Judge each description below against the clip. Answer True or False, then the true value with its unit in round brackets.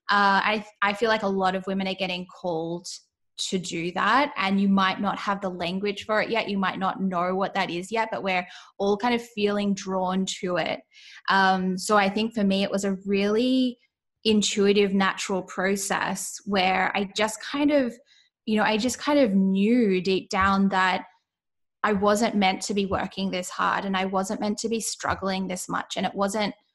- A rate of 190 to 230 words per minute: True (200 wpm)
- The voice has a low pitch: False (195 Hz)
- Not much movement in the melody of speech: True (2.1 semitones)